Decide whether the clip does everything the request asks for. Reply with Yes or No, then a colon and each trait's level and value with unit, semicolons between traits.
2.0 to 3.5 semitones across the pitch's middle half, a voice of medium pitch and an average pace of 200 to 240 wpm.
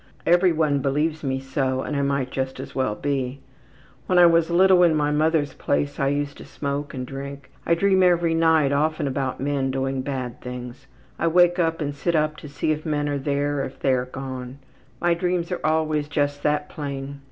Yes: average, 3.0 semitones; medium, 145 Hz; fast, 205 wpm